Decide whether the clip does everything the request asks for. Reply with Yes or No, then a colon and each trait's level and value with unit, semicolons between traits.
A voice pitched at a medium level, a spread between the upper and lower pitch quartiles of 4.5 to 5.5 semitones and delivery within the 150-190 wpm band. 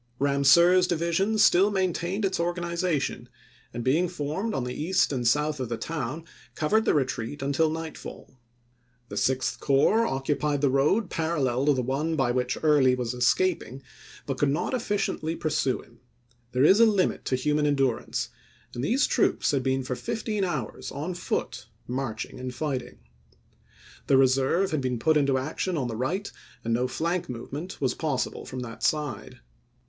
Yes: medium, 145 Hz; average, 4.9 semitones; average, 165 wpm